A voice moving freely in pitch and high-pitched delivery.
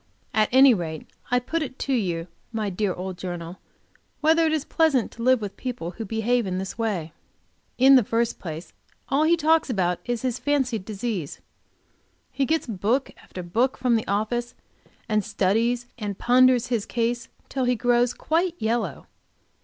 No: average, 4.5 semitones; high, 235 Hz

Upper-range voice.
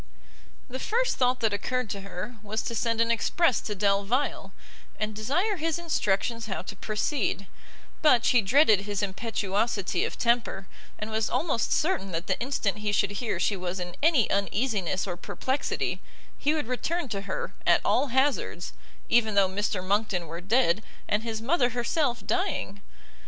Yes: high, 220 Hz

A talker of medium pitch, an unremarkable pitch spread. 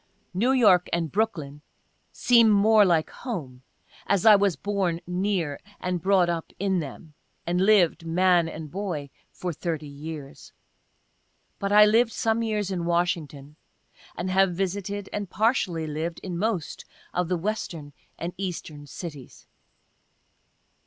Yes: medium, 180 Hz; average, 3.8 semitones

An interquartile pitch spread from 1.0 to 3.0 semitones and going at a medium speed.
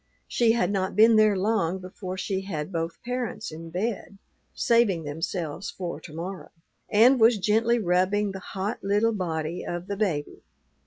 No: average, 3.8 semitones; average, 160 wpm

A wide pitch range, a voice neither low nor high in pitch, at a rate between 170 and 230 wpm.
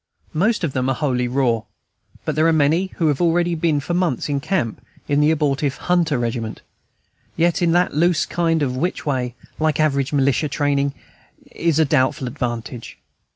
No: average, 4.0 semitones; medium, 145 Hz; average, 175 wpm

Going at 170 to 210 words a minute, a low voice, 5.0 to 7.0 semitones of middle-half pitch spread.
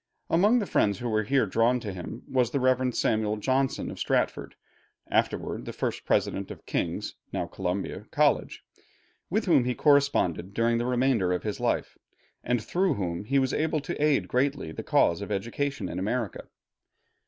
Yes: average, 175 wpm; low, 125 Hz; average, 5.3 semitones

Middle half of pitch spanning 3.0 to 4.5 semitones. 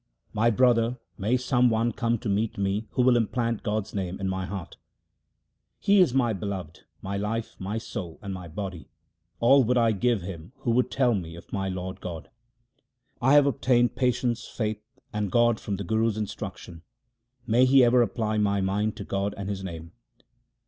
Yes: average, 3.7 semitones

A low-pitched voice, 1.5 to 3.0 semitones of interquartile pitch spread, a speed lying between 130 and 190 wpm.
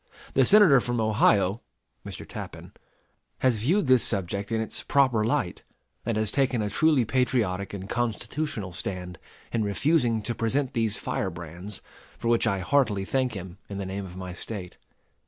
No: low, 110 Hz; average, 4.6 semitones; average, 160 wpm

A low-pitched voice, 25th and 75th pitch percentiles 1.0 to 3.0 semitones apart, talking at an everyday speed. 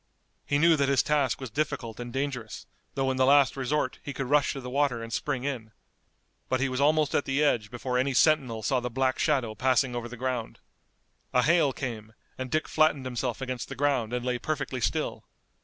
No: low, 130 Hz; narrow, 2.5 semitones; fast, 210 wpm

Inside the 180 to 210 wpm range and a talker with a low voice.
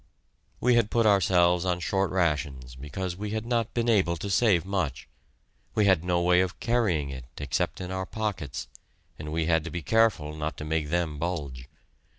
Yes: average, 185 wpm; very low, 90 Hz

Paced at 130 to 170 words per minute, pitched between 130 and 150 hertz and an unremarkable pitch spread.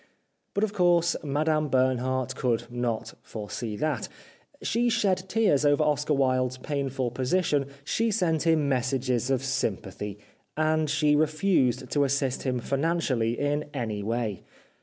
Yes: slow, 135 wpm; medium, 140 Hz; average, 3.8 semitones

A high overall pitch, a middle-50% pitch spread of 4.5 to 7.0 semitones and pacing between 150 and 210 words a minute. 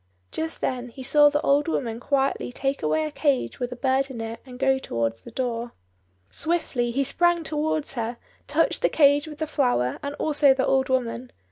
No: very high, 265 Hz; average, 3.3 semitones; average, 200 wpm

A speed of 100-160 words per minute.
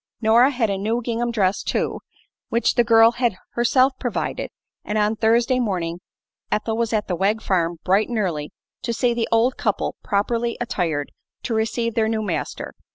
No: average, 175 wpm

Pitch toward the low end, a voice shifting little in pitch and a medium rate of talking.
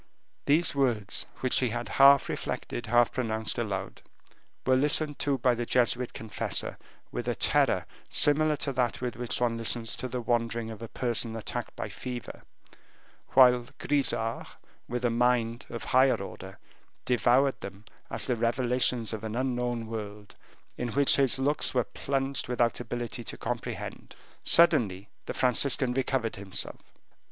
Yes: low, 120 Hz; narrow, 2.3 semitones; average, 150 wpm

